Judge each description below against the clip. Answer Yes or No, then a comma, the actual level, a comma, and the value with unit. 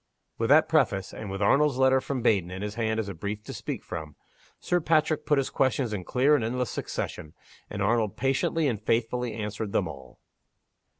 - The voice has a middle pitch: No, low, 110 Hz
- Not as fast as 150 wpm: No, average, 195 wpm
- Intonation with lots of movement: No, average, 4.7 semitones